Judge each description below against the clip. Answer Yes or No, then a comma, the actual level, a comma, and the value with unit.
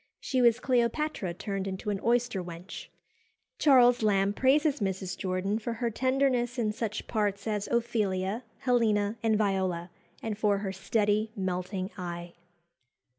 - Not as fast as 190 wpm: Yes, slow, 135 wpm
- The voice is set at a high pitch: Yes, high, 210 Hz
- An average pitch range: Yes, average, 3.7 semitones